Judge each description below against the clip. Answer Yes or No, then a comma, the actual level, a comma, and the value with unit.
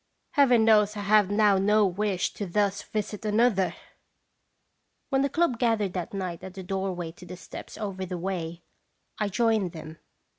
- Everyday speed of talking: Yes, average, 175 wpm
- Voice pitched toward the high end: Yes, high, 200 Hz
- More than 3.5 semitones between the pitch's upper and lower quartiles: No, average, 2.8 semitones